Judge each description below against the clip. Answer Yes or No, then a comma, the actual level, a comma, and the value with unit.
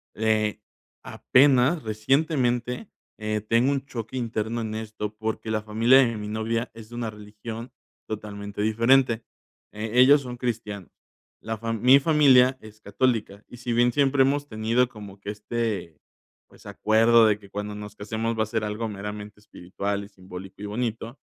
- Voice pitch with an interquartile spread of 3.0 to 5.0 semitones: No, narrow, 2.5 semitones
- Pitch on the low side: Yes, low, 110 Hz